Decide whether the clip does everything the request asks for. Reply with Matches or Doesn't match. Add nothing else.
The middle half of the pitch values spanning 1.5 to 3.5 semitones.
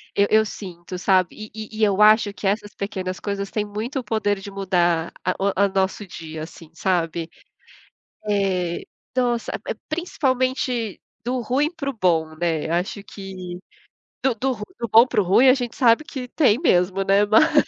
Doesn't match